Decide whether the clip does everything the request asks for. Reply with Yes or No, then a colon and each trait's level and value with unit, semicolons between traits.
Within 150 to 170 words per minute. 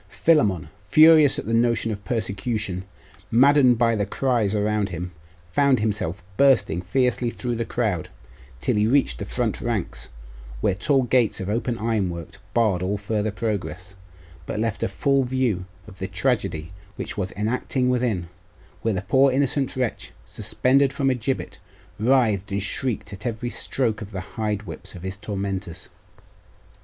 Yes: average, 155 wpm